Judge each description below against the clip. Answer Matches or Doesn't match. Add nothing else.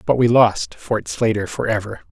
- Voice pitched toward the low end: Matches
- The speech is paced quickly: Doesn't match